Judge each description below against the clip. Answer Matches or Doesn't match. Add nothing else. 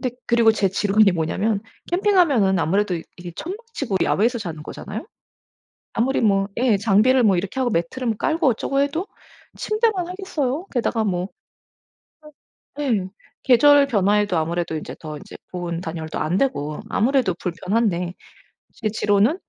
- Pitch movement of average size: Doesn't match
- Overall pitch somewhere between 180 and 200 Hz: Doesn't match